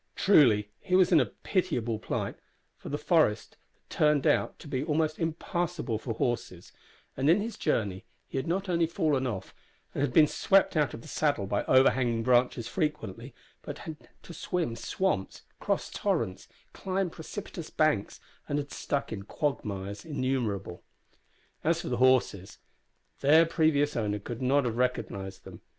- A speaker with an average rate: Yes, average, 160 wpm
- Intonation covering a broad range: Yes, wide, 5.9 semitones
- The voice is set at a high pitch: No, medium, 140 Hz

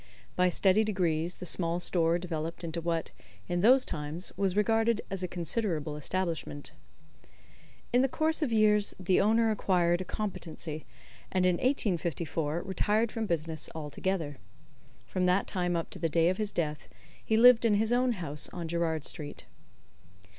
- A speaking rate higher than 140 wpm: Yes, average, 160 wpm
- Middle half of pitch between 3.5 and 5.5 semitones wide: Yes, average, 4.3 semitones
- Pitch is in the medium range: Yes, medium, 180 Hz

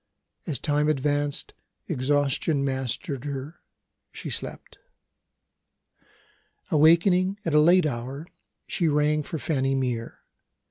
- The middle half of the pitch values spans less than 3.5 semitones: Yes, average, 2.7 semitones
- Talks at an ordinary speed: No, slow, 100 wpm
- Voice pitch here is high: No, medium, 145 Hz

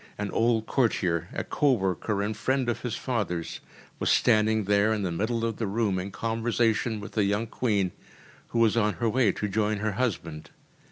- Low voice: Yes, low, 110 Hz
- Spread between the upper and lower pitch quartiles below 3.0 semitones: Yes, narrow, 2.4 semitones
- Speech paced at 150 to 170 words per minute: No, average, 190 wpm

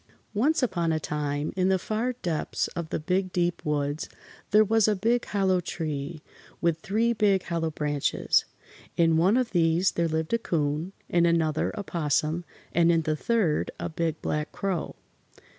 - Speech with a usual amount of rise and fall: Yes, average, 3.8 semitones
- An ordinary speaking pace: Yes, average, 170 wpm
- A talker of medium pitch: Yes, medium, 170 Hz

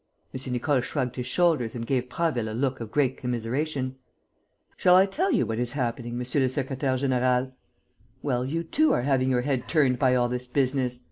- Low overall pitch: Yes, low, 130 Hz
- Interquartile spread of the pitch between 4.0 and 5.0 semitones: No, narrow, 2.4 semitones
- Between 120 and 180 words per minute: No, average, 195 wpm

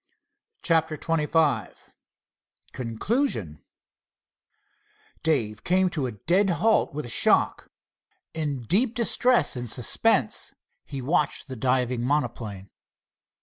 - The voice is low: No, medium, 145 Hz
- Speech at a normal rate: No, slow, 100 wpm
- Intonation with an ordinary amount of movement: No, wide, 5.9 semitones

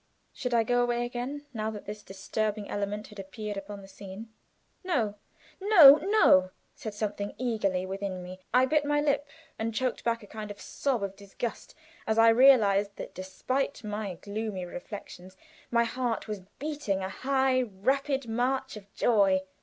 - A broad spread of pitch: No, average, 4.3 semitones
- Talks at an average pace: Yes, average, 170 wpm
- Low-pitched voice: No, high, 220 Hz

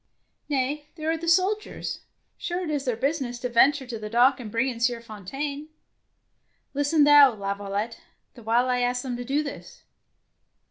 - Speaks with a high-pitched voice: Yes, very high, 260 Hz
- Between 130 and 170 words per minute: No, average, 180 wpm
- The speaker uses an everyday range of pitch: Yes, average, 3.9 semitones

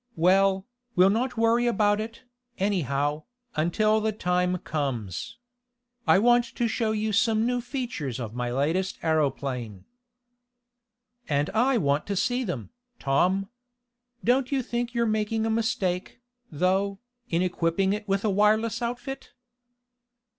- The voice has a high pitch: Yes, high, 200 Hz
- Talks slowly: Yes, slow, 130 wpm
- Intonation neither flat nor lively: No, wide, 5.9 semitones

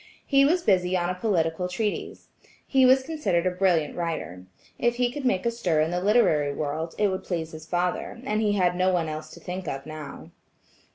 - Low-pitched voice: No, medium, 180 Hz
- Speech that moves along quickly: Yes, fast, 210 wpm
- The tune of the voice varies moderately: Yes, average, 5.0 semitones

